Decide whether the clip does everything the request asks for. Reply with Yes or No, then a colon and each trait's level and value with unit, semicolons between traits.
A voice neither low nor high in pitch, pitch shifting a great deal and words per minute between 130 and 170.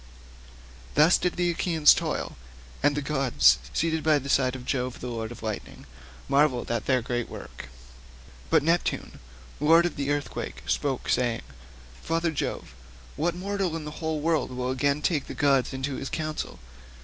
No: medium, 145 Hz; average, 4.0 semitones; average, 165 wpm